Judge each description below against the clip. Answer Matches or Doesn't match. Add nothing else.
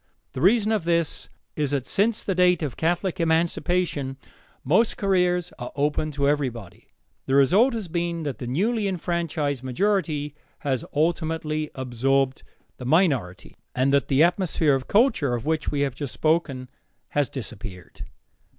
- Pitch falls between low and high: Matches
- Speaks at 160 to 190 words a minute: Doesn't match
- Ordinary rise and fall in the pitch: Matches